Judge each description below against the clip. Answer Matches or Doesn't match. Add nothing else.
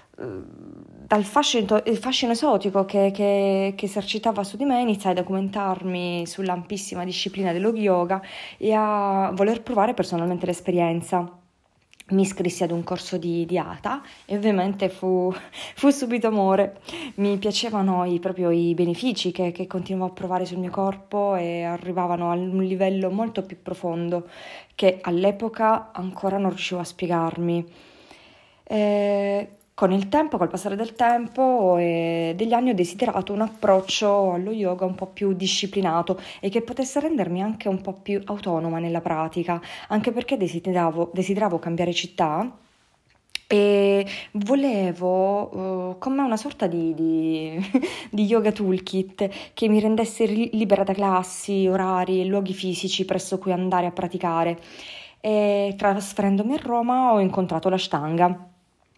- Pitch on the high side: Matches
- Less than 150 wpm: Matches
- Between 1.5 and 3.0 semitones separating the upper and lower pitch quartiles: Matches